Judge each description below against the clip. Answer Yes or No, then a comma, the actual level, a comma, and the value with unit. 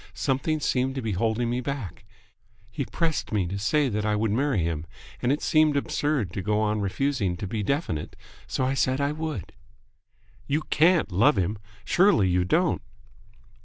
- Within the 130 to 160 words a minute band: No, average, 175 wpm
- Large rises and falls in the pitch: Yes, wide, 6.0 semitones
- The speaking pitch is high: No, low, 120 Hz